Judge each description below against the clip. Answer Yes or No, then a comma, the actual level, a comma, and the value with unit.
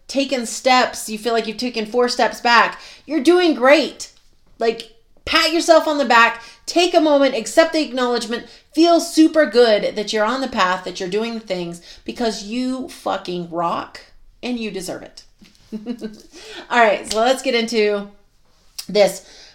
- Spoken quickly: No, average, 165 wpm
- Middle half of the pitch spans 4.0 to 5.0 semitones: Yes, average, 4.7 semitones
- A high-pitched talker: Yes, high, 235 Hz